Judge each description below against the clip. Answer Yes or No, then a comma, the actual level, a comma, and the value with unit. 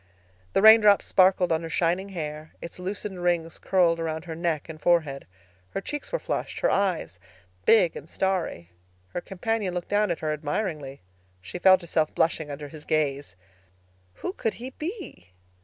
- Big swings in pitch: No, average, 4.0 semitones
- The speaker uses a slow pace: No, average, 165 wpm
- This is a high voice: No, medium, 170 Hz